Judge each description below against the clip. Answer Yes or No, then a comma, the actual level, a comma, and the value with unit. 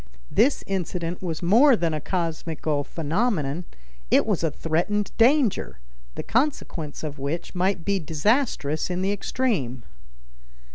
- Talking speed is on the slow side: Yes, slow, 130 wpm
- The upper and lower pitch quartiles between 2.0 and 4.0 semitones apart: No, average, 4.9 semitones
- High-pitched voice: No, medium, 175 Hz